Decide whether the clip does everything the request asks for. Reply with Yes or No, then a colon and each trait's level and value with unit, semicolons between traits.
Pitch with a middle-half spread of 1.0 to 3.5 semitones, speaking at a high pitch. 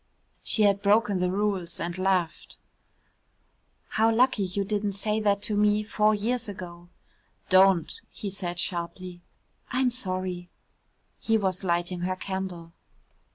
Yes: average, 2.7 semitones; high, 195 Hz